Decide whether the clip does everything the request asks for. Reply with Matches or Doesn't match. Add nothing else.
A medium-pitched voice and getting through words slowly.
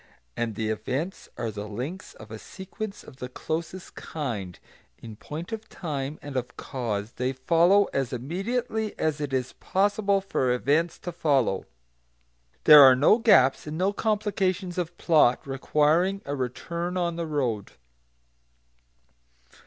Doesn't match